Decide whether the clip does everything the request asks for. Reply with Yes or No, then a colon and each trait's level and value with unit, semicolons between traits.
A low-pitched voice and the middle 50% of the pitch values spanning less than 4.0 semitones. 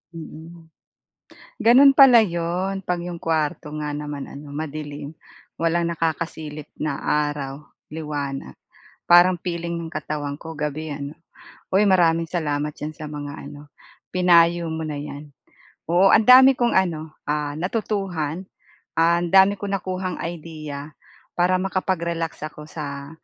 No: medium, 160 Hz; average, 3.0 semitones